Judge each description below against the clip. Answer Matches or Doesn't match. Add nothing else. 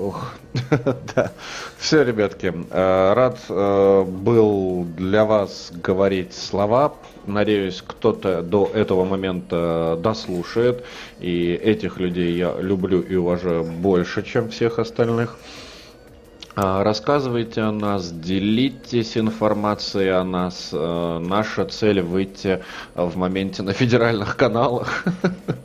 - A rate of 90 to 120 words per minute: Matches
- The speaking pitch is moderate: Doesn't match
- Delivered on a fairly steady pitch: Doesn't match